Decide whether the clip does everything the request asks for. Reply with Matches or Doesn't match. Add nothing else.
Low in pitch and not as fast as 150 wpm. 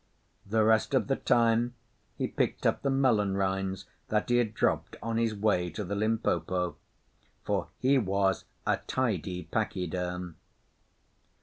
Matches